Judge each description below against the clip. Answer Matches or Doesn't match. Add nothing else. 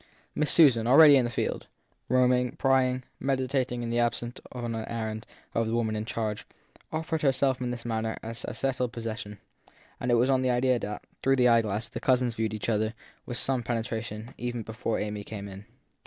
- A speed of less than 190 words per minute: Doesn't match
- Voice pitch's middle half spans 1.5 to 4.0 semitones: Matches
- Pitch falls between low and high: Doesn't match